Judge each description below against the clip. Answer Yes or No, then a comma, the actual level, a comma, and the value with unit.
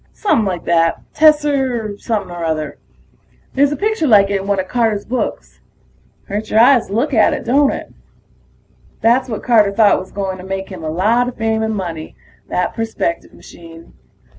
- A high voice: Yes, high, 215 Hz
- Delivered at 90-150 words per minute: No, average, 185 wpm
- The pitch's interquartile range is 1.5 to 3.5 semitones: No, average, 4.6 semitones